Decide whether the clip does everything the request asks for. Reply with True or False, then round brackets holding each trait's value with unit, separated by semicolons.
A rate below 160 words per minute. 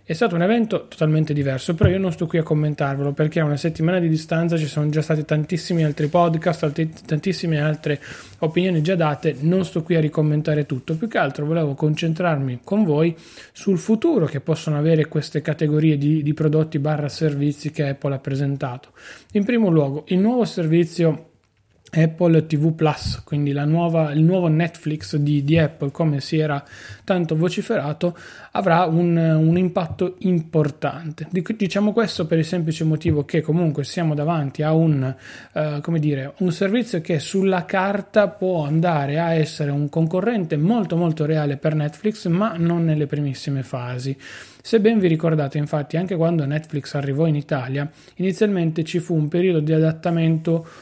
False (170 wpm)